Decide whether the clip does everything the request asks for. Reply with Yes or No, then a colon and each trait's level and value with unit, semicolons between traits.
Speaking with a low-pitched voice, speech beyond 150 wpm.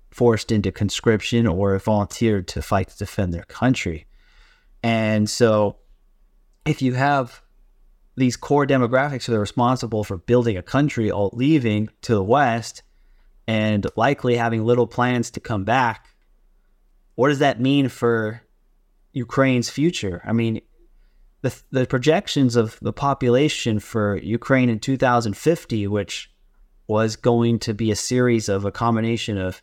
No: low, 115 Hz; average, 140 wpm